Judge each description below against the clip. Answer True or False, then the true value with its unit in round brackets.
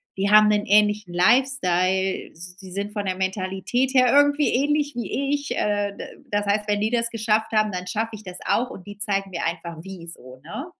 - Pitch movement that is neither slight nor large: True (3.7 semitones)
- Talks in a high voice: True (205 Hz)